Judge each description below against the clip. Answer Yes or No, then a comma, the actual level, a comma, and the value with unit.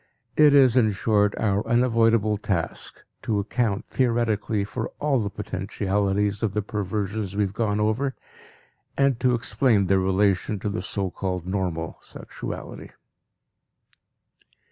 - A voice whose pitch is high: No, low, 105 Hz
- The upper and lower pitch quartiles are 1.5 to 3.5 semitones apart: Yes, average, 2.7 semitones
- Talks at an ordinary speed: No, slow, 130 wpm